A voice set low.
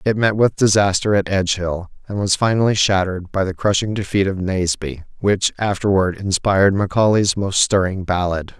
Yes: very low, 95 Hz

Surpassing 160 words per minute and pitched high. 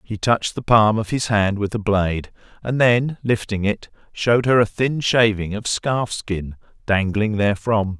No: average, 180 wpm; low, 105 Hz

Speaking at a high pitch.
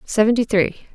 Yes: high, 215 Hz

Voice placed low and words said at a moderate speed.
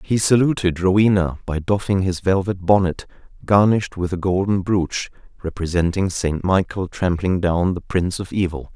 Yes: very low, 95 Hz; average, 150 wpm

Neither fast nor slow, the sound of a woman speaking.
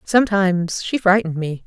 Yes: average, 145 wpm; female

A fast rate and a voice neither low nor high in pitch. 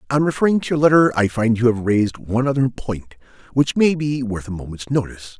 No: fast, 220 wpm; low, 125 Hz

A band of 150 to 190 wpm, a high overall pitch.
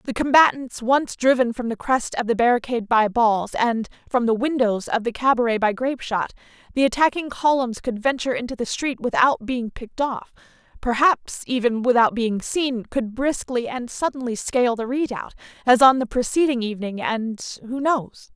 Yes: average, 175 wpm; high, 245 Hz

